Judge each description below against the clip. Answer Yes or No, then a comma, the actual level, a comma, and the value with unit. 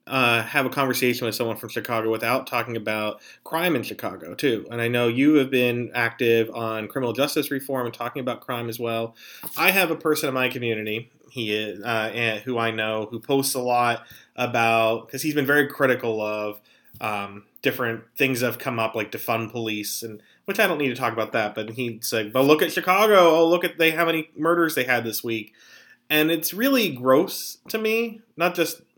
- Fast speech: Yes, fast, 210 wpm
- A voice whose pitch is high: No, low, 120 Hz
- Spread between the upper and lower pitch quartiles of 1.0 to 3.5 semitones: No, average, 4.2 semitones